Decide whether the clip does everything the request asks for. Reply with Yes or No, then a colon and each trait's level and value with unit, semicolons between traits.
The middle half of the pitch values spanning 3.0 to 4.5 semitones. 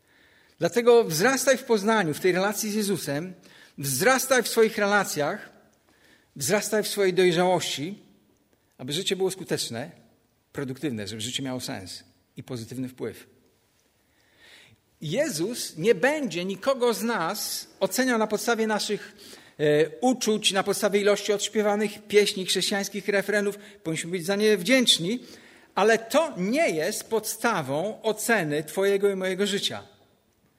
No: average, 5.0 semitones